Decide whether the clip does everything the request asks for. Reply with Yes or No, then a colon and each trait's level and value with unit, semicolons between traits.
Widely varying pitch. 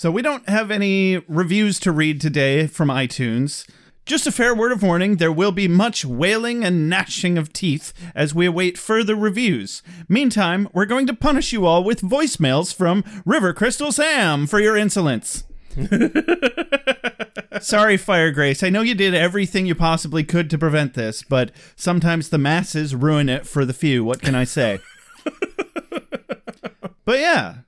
Yes: wide, 5.8 semitones